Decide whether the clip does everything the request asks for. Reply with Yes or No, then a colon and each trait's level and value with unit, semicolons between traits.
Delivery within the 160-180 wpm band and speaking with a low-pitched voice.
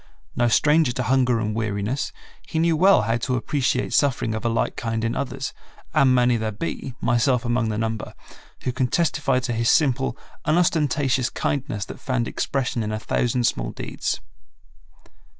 Yes: average, 170 wpm; low, 125 Hz